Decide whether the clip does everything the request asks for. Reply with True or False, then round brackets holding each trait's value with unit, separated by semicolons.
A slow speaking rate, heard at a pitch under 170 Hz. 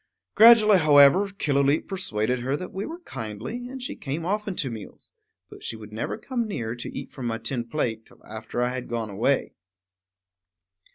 False (180 wpm; 135 Hz)